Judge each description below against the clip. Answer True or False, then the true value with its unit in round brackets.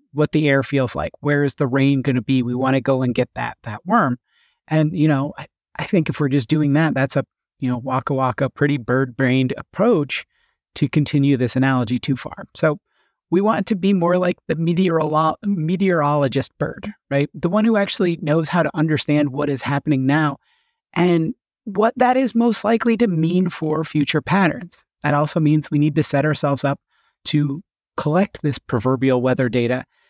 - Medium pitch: True (150 Hz)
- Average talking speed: True (195 wpm)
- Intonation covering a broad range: False (4.1 semitones)